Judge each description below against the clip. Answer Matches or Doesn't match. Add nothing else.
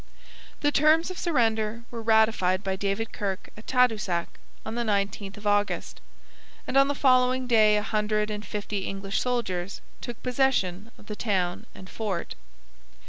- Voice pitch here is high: Matches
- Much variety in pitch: Doesn't match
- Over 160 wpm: Doesn't match